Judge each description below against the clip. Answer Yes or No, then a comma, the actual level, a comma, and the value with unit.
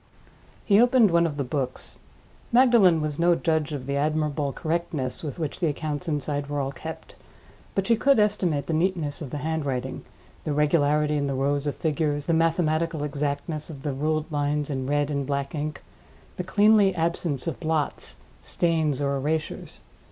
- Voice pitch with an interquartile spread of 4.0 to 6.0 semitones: No, narrow, 2.6 semitones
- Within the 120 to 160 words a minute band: No, average, 175 wpm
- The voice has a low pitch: No, medium, 150 Hz